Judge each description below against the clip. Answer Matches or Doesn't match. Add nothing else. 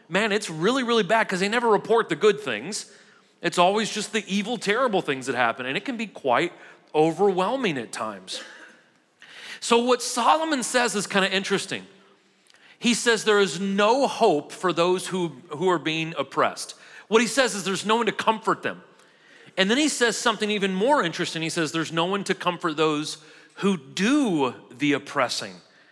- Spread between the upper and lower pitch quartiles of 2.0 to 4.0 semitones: Doesn't match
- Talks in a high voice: Matches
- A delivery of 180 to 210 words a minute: Matches